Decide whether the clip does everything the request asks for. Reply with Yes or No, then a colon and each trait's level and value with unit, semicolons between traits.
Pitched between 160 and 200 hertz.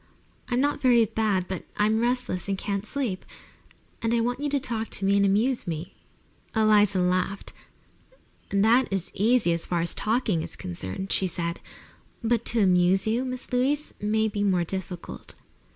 No: high, 210 Hz